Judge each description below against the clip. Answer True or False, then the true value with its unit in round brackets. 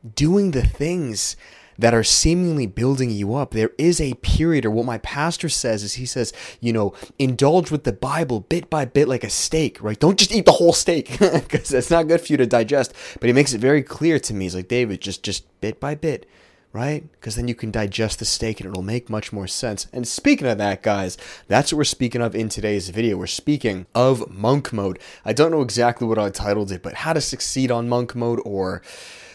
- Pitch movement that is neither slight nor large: False (5.7 semitones)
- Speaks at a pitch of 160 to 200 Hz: False (120 Hz)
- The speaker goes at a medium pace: False (230 wpm)